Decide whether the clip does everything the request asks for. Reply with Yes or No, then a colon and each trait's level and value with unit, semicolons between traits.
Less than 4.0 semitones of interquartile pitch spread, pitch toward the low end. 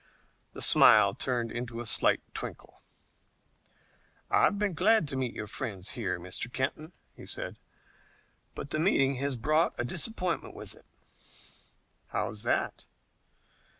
No: average, 5.1 semitones; low, 130 Hz